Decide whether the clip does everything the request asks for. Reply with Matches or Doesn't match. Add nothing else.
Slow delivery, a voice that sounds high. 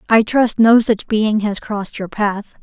Doesn't match